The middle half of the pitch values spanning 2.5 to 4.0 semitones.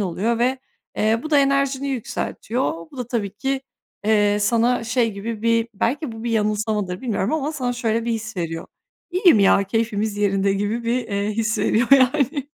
Yes: average, 3.7 semitones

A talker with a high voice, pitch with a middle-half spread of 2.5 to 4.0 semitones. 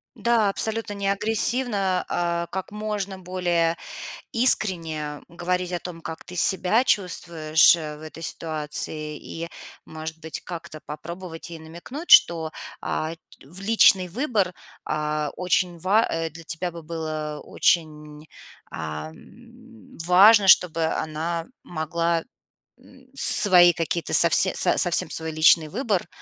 No: medium, 170 Hz; average, 3.5 semitones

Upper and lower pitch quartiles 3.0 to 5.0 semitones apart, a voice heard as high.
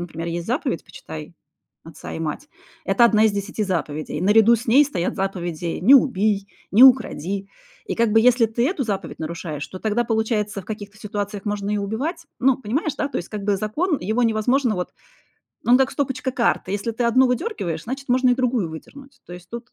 Yes: average, 4.7 semitones; high, 215 Hz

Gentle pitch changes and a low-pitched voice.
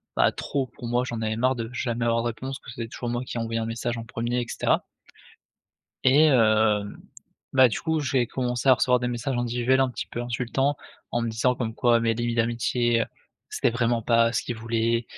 Yes: narrow, 1.5 semitones; low, 120 Hz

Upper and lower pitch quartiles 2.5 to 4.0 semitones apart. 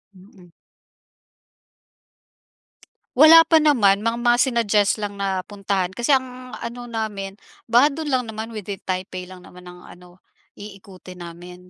No: average, 4.6 semitones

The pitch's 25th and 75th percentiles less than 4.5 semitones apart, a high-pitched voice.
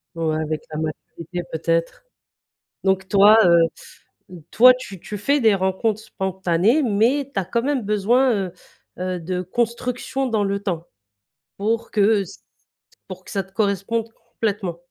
Yes: average, 3.9 semitones; high, 200 Hz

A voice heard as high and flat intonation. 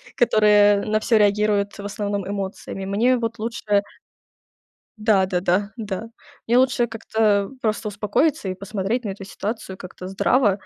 Yes: high, 205 Hz; narrow, 2.0 semitones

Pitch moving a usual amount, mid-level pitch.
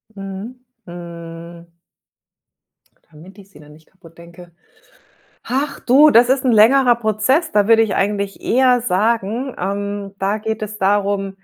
No: average, 4.1 semitones; high, 205 Hz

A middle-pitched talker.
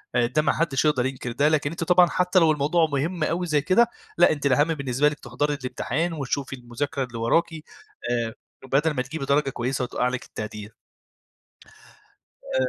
Yes: medium, 145 Hz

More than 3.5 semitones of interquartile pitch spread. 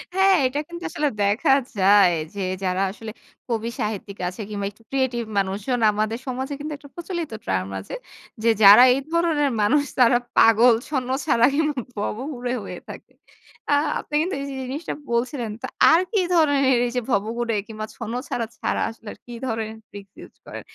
Yes: average, 4.7 semitones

